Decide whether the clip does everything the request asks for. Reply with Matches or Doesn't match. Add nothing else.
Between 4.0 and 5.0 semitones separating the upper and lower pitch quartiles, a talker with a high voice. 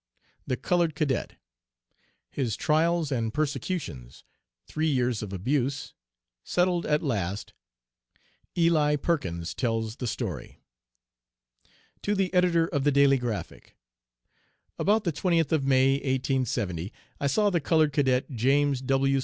Doesn't match